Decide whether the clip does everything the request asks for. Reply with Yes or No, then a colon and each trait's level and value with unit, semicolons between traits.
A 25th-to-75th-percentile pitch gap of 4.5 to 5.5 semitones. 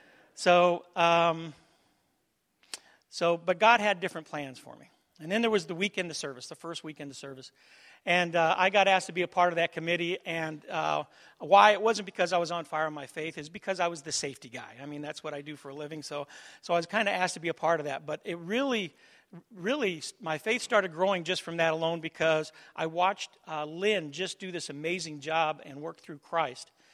No: average, 3.4 semitones